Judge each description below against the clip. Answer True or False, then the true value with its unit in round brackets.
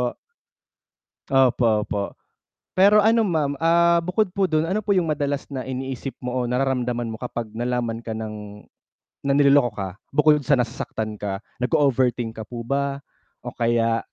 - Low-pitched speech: True (130 Hz)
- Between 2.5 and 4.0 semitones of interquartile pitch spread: False (4.7 semitones)